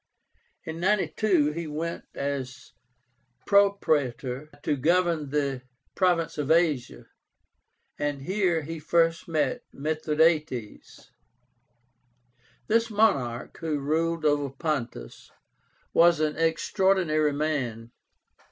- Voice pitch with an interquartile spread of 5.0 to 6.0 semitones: No, average, 3.1 semitones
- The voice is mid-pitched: Yes, medium, 155 Hz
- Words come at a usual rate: No, slow, 90 wpm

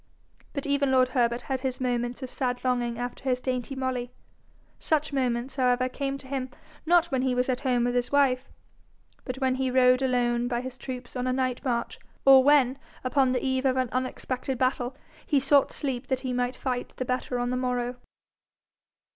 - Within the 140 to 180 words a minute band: No, average, 195 wpm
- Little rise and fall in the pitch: Yes, narrow, 1.2 semitones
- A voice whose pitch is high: Yes, very high, 255 Hz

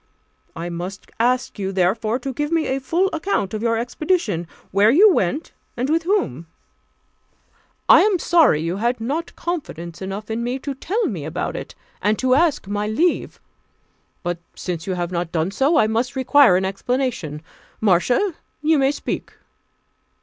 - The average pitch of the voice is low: No, high, 235 Hz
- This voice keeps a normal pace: Yes, average, 165 wpm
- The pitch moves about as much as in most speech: No, wide, 7.9 semitones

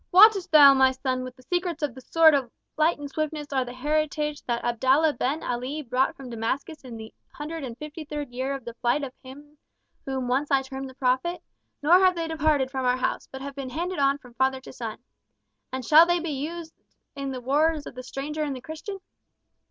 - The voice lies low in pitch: No, very high, 275 Hz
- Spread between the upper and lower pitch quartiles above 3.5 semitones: No, average, 3.2 semitones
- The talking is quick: Yes, fast, 220 wpm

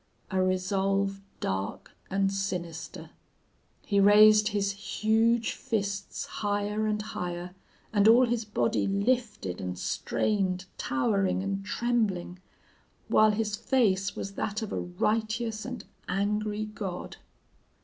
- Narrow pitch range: Yes, narrow, 2.2 semitones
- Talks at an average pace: No, slow, 115 wpm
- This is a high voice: Yes, high, 205 Hz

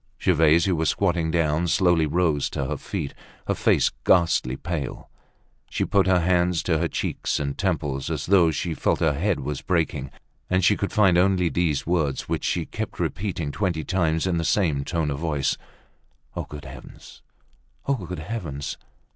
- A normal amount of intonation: Yes, average, 3.3 semitones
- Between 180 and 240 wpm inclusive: No, average, 170 wpm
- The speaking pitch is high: No, very low, 85 Hz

